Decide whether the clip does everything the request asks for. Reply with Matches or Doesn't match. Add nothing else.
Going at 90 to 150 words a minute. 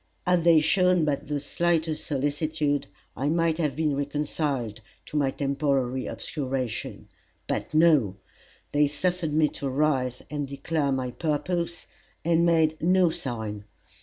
Matches